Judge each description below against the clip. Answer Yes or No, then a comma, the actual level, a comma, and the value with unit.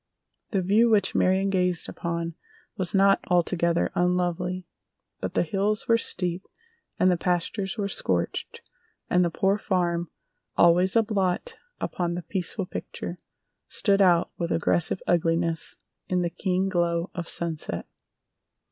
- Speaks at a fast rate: No, slow, 135 wpm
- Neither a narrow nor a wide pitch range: No, narrow, 2.0 semitones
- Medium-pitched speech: Yes, medium, 180 Hz